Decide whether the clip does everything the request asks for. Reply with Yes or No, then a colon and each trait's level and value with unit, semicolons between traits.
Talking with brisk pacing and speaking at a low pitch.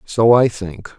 No: average, 185 wpm; low, 110 Hz